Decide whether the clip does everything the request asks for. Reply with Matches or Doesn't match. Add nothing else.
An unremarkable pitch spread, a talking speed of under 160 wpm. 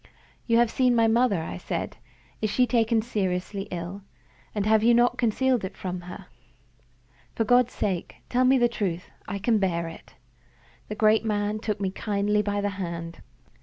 Doesn't match